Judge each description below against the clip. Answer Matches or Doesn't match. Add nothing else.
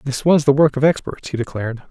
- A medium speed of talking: Doesn't match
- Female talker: Doesn't match